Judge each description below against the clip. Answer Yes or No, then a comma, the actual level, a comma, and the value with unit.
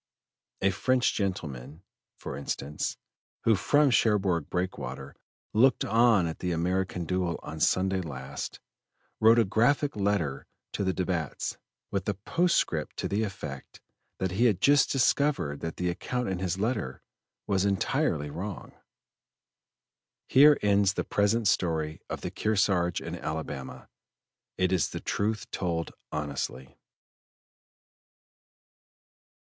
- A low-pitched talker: Yes, very low, 95 Hz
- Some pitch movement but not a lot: Yes, average, 4.7 semitones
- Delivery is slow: Yes, slow, 125 wpm